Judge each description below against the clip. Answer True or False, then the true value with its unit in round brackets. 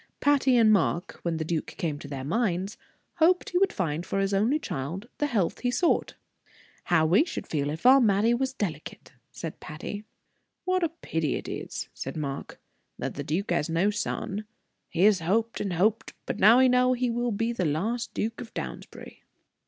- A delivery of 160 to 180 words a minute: False (190 wpm)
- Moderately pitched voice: False (205 Hz)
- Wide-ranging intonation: True (6.8 semitones)